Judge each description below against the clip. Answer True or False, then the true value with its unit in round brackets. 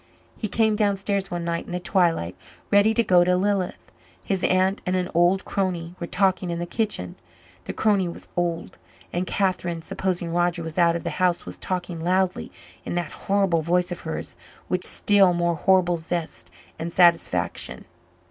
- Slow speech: False (175 wpm)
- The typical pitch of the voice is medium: True (180 Hz)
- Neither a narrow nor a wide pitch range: False (2.0 semitones)